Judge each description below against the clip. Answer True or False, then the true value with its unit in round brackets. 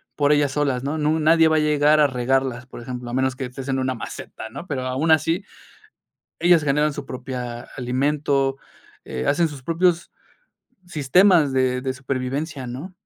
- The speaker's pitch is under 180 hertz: True (140 Hz)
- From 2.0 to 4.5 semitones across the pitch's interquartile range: True (2.9 semitones)